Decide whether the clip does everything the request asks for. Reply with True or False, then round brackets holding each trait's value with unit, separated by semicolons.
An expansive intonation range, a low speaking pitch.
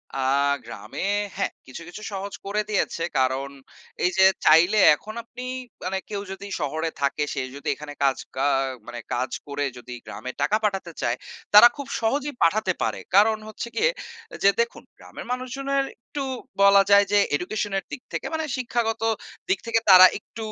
False (7.4 semitones; 195 Hz)